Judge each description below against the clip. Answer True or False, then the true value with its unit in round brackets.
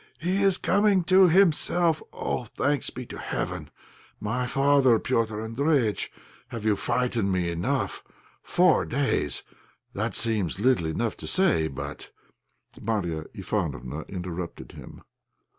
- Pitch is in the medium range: False (120 Hz)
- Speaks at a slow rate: True (125 wpm)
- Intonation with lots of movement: True (8.1 semitones)